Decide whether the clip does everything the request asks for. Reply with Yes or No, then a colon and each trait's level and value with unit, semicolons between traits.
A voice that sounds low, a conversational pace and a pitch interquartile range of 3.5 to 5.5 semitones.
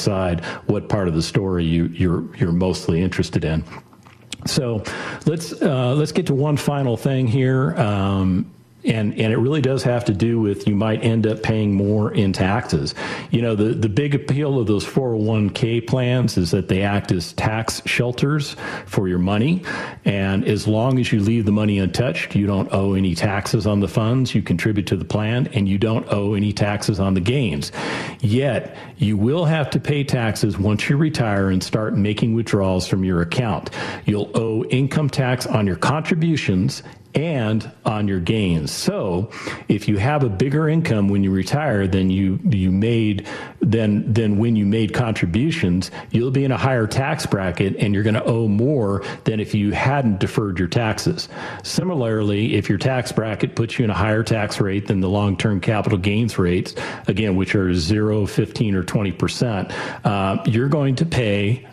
Yes: low, 110 Hz; average, 185 wpm; average, 4.3 semitones